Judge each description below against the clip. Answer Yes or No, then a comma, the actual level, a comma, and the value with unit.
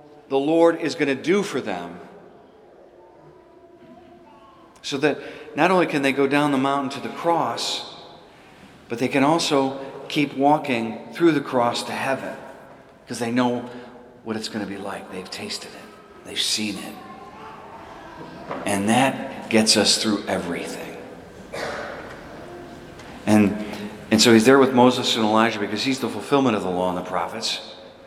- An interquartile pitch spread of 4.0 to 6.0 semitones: Yes, average, 4.6 semitones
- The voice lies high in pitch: No, low, 120 Hz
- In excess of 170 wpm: No, average, 155 wpm